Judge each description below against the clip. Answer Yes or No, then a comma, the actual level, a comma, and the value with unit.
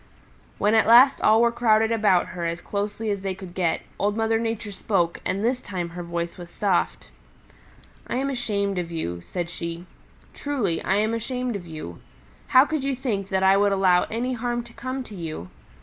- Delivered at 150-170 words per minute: No, average, 195 wpm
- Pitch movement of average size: Yes, average, 4.8 semitones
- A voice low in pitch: No, high, 205 Hz